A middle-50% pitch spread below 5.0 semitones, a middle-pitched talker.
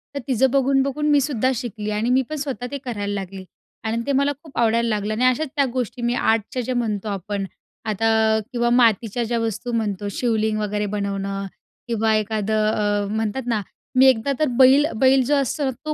No: average, 3.6 semitones; high, 230 Hz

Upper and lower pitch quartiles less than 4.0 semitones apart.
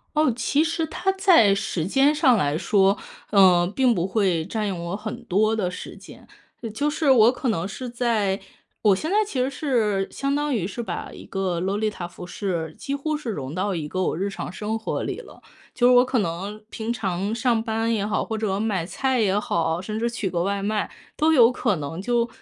No: average, 4.7 semitones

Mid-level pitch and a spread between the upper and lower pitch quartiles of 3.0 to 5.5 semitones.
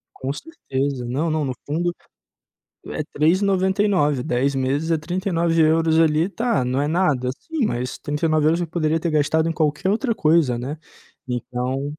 Yes: medium, 155 Hz; average, 3.9 semitones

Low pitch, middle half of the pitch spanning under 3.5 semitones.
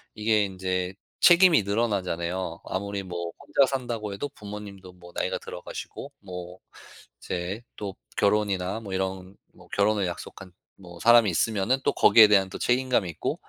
Yes: low, 100 Hz; average, 2.8 semitones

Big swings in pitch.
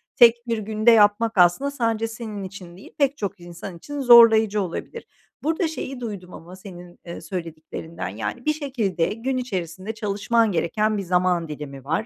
No: average, 5.0 semitones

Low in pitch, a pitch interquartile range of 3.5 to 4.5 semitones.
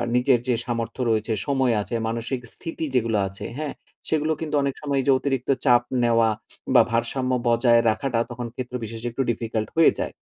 No: low, 120 Hz; average, 2.8 semitones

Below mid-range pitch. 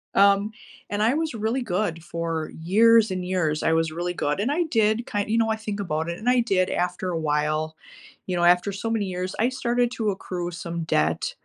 No: medium, 185 Hz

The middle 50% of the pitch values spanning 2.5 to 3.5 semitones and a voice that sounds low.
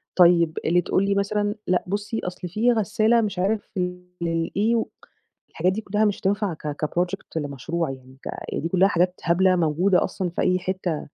No: average, 3.2 semitones; medium, 185 Hz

